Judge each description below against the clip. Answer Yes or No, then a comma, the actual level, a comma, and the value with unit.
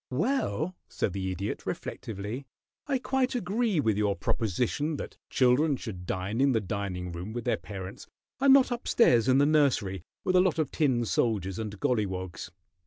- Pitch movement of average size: No, wide, 8.0 semitones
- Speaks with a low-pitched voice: Yes, low, 120 Hz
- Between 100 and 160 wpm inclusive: No, average, 175 wpm